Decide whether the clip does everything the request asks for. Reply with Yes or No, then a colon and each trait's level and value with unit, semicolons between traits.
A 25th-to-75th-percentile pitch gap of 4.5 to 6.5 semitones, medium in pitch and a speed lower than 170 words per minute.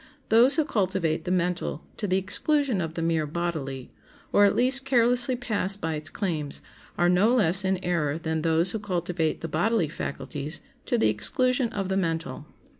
No: wide, 5.4 semitones; medium, 180 Hz; average, 180 wpm